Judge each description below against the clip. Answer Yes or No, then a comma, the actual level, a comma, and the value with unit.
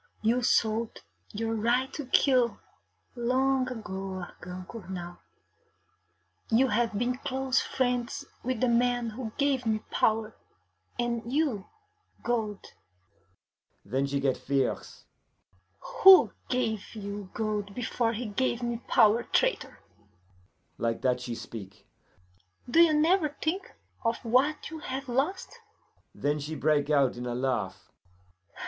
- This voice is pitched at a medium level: No, high, 230 Hz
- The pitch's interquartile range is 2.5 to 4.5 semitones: No, average, 5.1 semitones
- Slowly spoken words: Yes, slow, 125 wpm